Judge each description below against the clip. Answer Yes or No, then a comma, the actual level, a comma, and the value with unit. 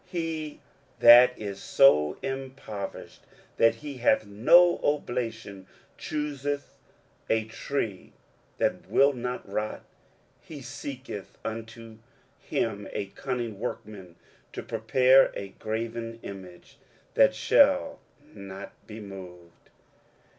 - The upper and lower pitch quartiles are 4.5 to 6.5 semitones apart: Yes, average, 5.2 semitones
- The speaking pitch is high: No, low, 115 Hz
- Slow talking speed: Yes, slow, 105 wpm